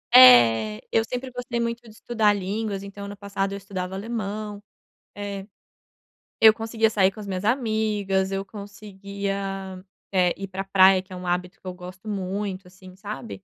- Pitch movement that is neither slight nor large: No, narrow, 2.2 semitones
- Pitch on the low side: No, high, 200 Hz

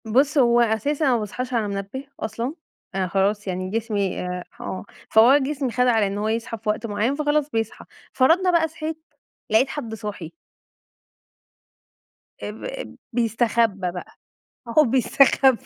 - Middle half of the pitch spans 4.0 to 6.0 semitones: Yes, average, 4.7 semitones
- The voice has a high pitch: Yes, high, 230 Hz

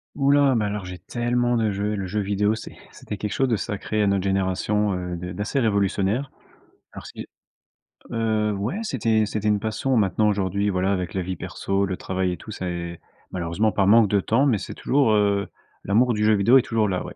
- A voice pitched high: No, low, 105 Hz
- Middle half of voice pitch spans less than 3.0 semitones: Yes, narrow, 2.5 semitones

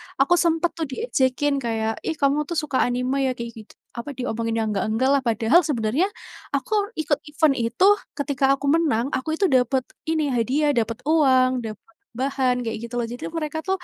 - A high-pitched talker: Yes, very high, 265 Hz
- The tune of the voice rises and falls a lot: No, average, 4.3 semitones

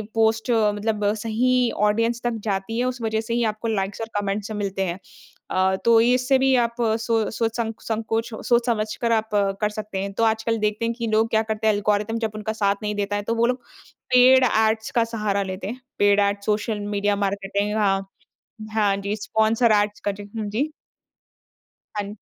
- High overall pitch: Yes, high, 220 Hz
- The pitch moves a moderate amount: No, narrow, 2.0 semitones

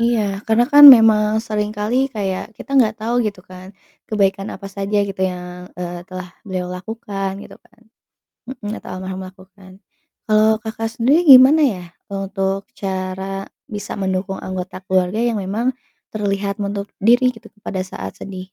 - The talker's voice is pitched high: Yes, high, 200 Hz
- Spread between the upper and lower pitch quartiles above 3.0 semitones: No, average, 2.7 semitones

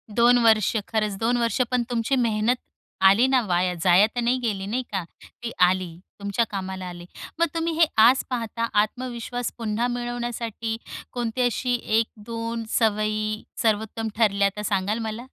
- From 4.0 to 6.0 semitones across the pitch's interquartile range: No, average, 2.7 semitones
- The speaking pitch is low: No, high, 225 Hz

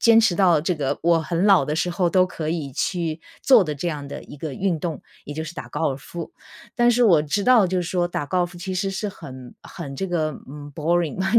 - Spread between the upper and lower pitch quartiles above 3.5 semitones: Yes, average, 3.9 semitones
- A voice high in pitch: No, medium, 170 Hz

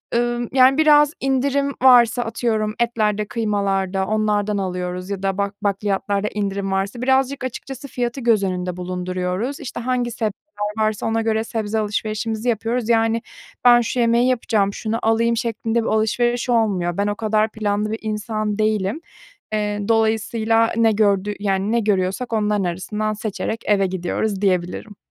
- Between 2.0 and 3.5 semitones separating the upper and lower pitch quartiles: Yes, average, 2.7 semitones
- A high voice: Yes, high, 215 Hz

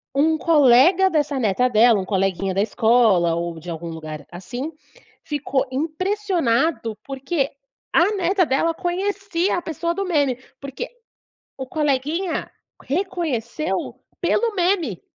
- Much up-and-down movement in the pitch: Yes, wide, 7.3 semitones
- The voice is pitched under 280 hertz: No, very high, 285 Hz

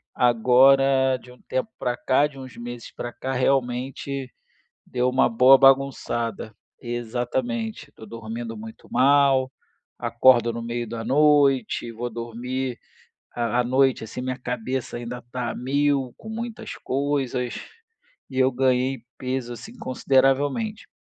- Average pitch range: No, narrow, 2.1 semitones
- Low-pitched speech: Yes, low, 125 Hz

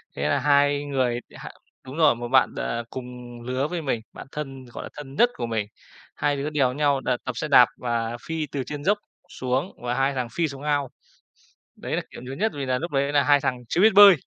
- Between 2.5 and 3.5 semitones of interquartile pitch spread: Yes, average, 2.9 semitones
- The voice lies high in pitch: No, low, 135 Hz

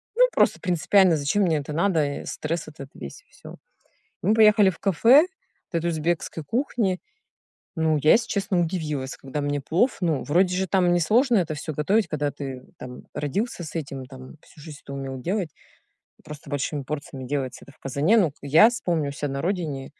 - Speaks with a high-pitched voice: No, medium, 155 Hz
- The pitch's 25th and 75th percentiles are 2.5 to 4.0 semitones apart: No, average, 4.9 semitones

